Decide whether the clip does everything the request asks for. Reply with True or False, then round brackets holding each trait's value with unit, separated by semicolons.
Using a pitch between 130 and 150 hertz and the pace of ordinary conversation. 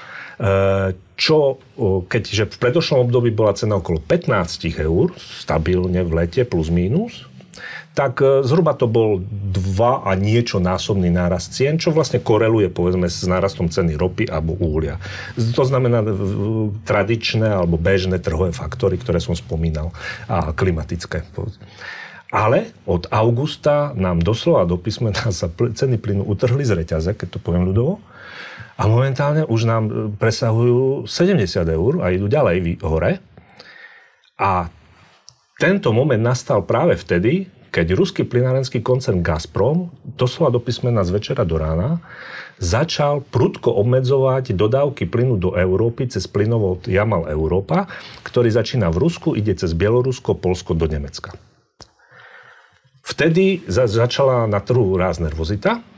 False (110 Hz; 130 wpm)